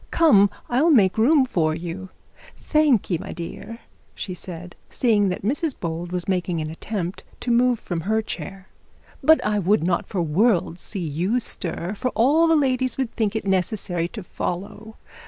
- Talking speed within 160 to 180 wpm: Yes, average, 175 wpm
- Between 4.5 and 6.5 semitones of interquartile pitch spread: Yes, wide, 5.4 semitones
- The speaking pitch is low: No, high, 200 Hz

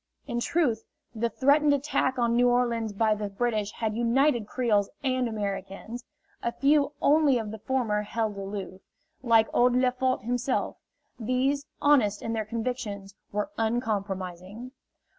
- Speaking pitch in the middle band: No, high, 235 Hz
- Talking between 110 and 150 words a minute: Yes, average, 140 wpm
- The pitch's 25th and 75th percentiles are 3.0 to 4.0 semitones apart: Yes, average, 3.4 semitones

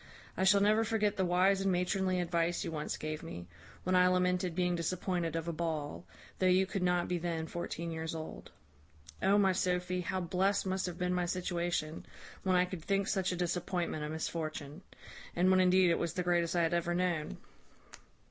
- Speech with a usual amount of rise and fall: No, narrow, 1.7 semitones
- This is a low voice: No, medium, 180 Hz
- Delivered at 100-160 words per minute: No, average, 195 wpm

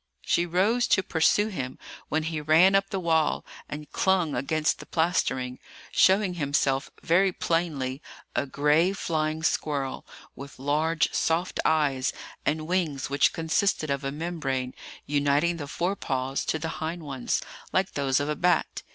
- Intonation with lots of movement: No, average, 3.6 semitones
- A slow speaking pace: No, average, 150 wpm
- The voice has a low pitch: No, medium, 155 Hz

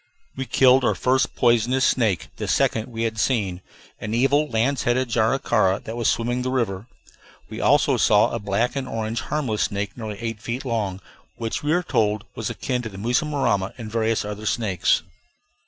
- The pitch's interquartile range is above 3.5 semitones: No, average, 3.1 semitones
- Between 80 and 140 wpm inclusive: No, average, 180 wpm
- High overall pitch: No, low, 115 Hz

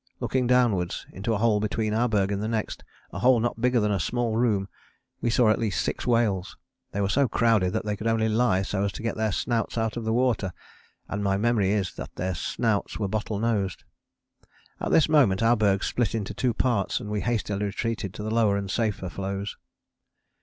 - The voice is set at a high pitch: No, low, 110 Hz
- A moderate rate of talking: No, fast, 215 wpm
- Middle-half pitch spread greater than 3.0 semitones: No, average, 2.7 semitones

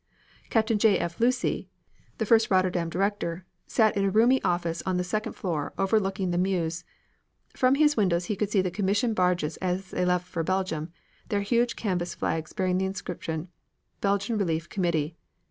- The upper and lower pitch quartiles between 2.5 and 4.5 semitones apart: Yes, average, 3.2 semitones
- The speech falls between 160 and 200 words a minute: Yes, average, 170 wpm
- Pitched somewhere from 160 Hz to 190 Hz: Yes, medium, 185 Hz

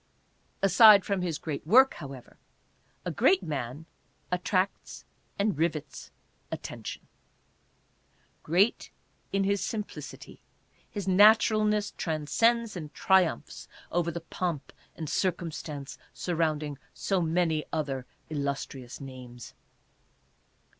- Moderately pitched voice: Yes, medium, 170 Hz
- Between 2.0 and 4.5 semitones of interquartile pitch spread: No, average, 5.0 semitones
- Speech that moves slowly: Yes, slow, 100 wpm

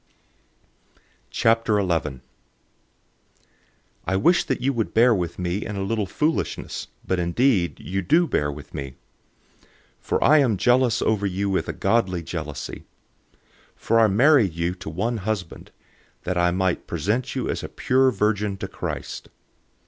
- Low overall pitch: Yes, low, 100 Hz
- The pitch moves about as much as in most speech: Yes, average, 4.7 semitones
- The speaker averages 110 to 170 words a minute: Yes, average, 150 wpm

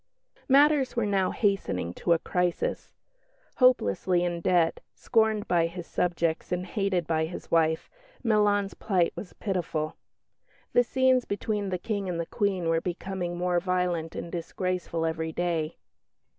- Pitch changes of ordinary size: Yes, average, 3.3 semitones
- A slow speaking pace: No, average, 145 wpm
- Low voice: No, medium, 180 Hz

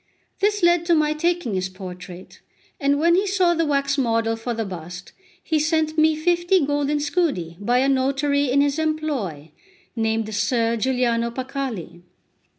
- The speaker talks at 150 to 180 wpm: Yes, average, 155 wpm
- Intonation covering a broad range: Yes, wide, 5.7 semitones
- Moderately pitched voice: No, very high, 275 Hz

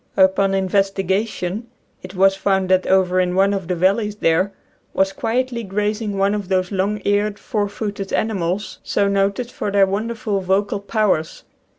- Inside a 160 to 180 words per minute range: Yes, average, 165 wpm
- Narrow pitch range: Yes, narrow, 1.7 semitones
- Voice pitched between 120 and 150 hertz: No, high, 195 Hz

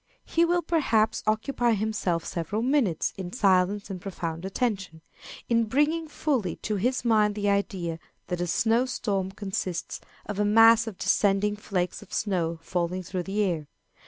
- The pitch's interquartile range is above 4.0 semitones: No, average, 3.7 semitones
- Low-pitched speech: No, high, 205 Hz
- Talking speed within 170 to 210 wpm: No, average, 160 wpm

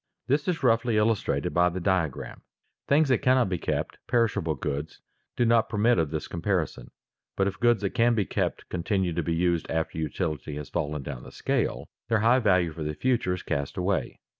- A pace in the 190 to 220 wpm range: Yes, average, 195 wpm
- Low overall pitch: Yes, very low, 95 Hz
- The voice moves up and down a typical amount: No, wide, 6.2 semitones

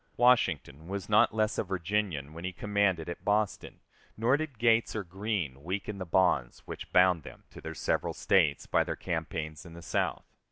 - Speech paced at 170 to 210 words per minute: Yes, average, 185 wpm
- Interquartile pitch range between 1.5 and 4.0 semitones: No, average, 4.5 semitones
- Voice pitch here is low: Yes, very low, 95 Hz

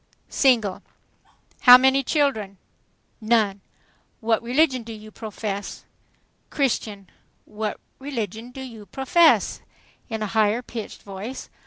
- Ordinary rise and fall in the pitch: Yes, average, 3.7 semitones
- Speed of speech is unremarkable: No, slow, 110 wpm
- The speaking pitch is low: No, high, 225 Hz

